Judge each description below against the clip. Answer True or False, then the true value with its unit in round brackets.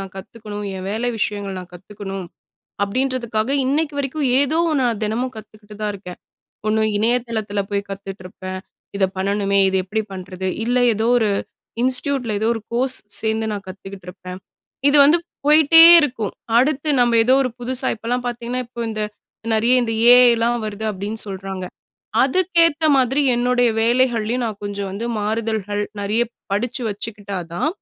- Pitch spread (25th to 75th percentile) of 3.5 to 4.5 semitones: True (3.8 semitones)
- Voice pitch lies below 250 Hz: True (220 Hz)